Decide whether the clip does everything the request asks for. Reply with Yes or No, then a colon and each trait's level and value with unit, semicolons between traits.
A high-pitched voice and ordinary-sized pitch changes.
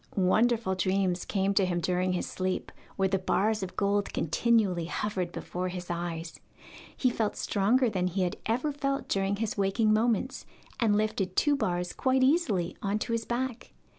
Yes: high, 200 Hz; average, 3.9 semitones